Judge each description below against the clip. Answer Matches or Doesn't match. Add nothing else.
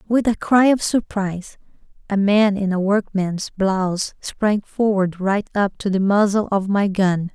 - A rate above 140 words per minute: Matches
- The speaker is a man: Doesn't match